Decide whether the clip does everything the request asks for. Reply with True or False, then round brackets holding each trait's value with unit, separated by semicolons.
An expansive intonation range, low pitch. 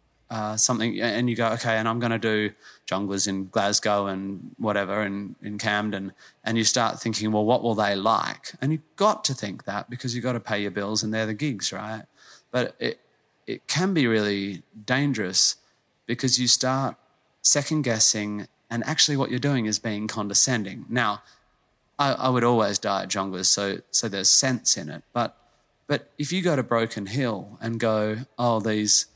False (3.2 semitones; 110 Hz)